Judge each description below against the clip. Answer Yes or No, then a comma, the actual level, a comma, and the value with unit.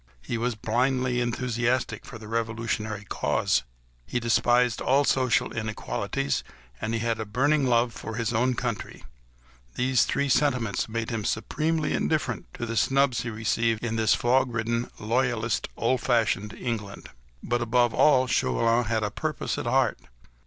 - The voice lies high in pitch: No, low, 120 Hz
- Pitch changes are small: Yes, narrow, 2.1 semitones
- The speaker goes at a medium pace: Yes, average, 150 wpm